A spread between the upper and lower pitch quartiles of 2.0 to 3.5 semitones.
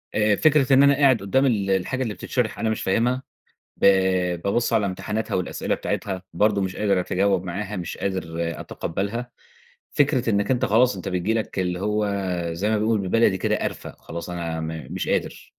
No: average, 4.0 semitones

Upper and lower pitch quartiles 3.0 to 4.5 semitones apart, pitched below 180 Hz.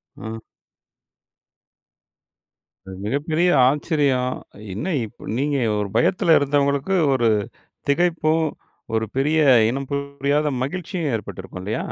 Yes: average, 3.8 semitones; medium, 140 Hz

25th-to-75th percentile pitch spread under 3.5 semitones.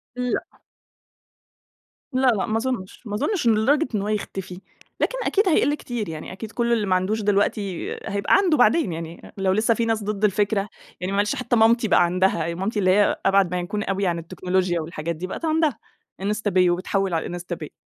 No: average, 3.8 semitones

